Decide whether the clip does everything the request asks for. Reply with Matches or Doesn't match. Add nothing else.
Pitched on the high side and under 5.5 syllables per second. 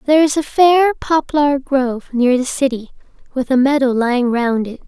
Matches